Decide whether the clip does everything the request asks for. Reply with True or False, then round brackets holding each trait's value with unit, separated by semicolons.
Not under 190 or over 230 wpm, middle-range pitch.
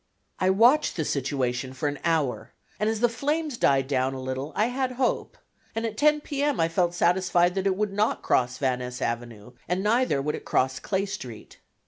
True (205 wpm; 175 Hz)